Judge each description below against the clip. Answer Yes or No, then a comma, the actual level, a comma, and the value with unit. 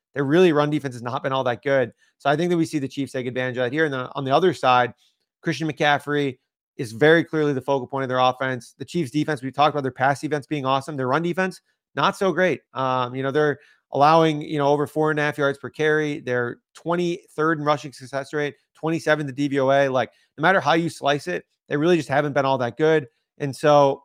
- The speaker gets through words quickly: Yes, fast, 250 wpm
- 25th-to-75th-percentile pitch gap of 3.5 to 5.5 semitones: No, average, 2.7 semitones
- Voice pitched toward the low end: No, medium, 145 Hz